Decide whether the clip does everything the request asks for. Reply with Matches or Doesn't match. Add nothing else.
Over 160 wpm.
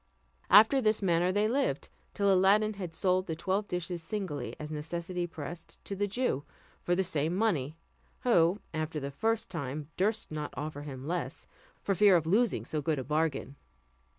Matches